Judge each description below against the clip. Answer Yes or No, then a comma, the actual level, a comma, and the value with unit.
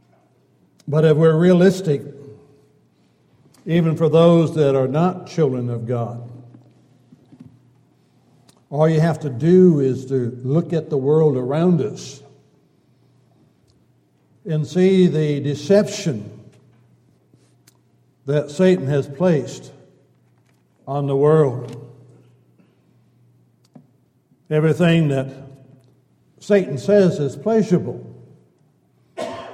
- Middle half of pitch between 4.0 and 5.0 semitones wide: Yes, average, 4.6 semitones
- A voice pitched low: No, medium, 145 Hz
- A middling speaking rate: No, slow, 85 wpm